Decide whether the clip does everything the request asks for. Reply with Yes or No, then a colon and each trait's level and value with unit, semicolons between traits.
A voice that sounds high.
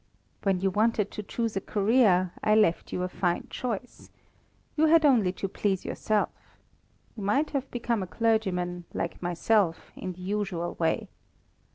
Yes: high, 200 Hz